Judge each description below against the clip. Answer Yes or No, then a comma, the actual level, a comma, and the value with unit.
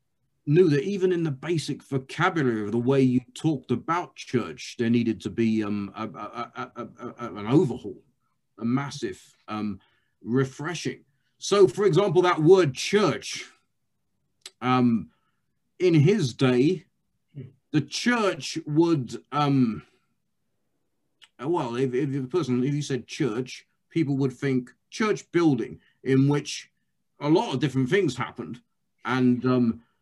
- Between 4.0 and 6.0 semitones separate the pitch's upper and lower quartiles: Yes, average, 4.6 semitones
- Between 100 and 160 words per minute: Yes, slow, 135 wpm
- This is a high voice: No, low, 135 Hz